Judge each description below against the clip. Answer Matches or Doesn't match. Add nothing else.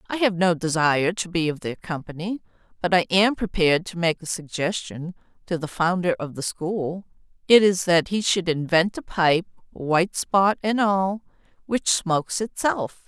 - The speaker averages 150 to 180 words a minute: Matches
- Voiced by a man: Doesn't match